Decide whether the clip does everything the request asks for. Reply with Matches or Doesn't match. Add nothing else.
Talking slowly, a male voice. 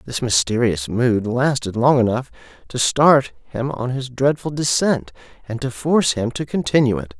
Doesn't match